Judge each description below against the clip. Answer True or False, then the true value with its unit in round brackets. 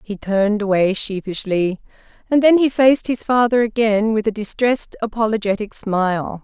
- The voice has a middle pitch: False (215 Hz)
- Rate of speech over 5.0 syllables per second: True (5.2 syllables/s)